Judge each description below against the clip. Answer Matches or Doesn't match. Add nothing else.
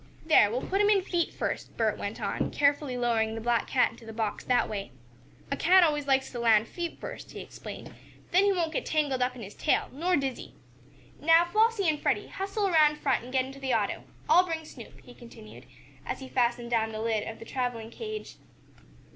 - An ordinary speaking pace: Doesn't match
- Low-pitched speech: Doesn't match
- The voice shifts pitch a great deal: Matches